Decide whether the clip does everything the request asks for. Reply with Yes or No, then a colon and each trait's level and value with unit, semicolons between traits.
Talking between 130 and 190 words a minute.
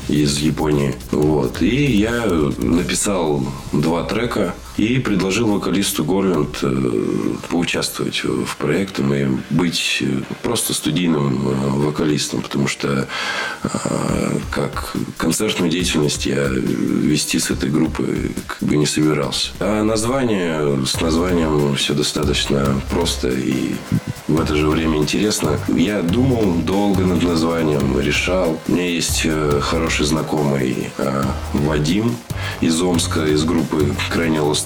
No: average, 115 wpm